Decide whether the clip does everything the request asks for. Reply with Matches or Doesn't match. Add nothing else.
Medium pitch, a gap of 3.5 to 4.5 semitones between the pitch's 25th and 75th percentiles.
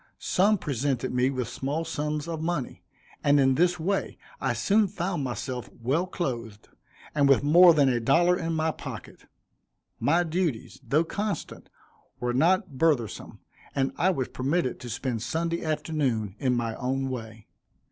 Doesn't match